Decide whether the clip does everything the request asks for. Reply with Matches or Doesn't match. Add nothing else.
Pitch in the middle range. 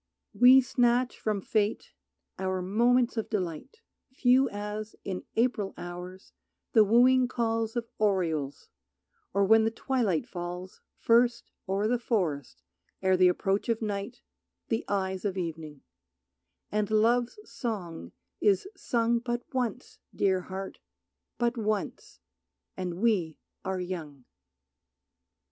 Doesn't match